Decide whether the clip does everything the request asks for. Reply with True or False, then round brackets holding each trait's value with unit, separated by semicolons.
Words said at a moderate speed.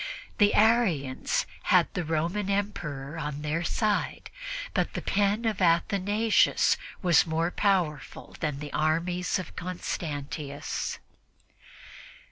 False (105 wpm)